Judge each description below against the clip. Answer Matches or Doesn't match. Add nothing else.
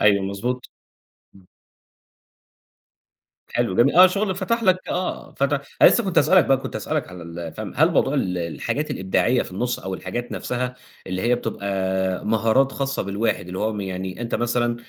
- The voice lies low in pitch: Matches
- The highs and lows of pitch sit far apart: Matches